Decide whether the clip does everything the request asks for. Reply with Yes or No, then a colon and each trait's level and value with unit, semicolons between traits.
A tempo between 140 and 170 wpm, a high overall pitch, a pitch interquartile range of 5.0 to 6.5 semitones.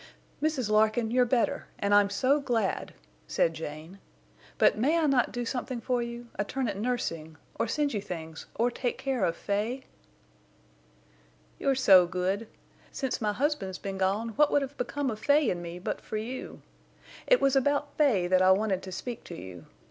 No: average, 180 wpm; high, 225 Hz; wide, 5.6 semitones